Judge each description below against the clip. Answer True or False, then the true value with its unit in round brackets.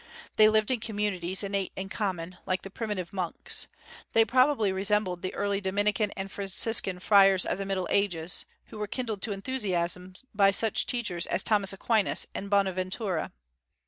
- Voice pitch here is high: True (195 Hz)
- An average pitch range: False (2.2 semitones)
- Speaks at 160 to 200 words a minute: True (165 wpm)